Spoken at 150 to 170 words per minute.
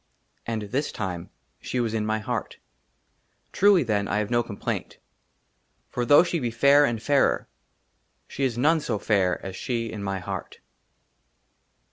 Yes: average, 155 wpm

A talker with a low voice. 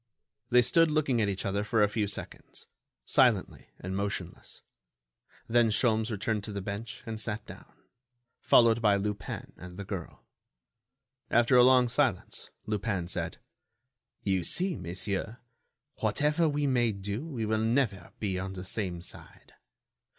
Yes: low, 110 Hz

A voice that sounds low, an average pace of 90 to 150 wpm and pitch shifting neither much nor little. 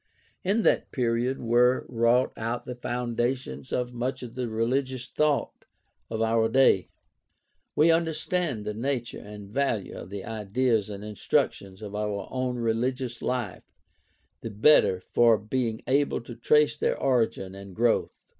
Yes: low, 120 Hz; average, 145 wpm; average, 3.1 semitones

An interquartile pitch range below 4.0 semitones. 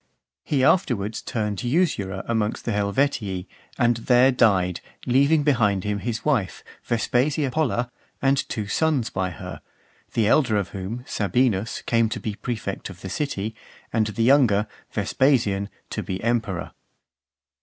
No: average, 4.3 semitones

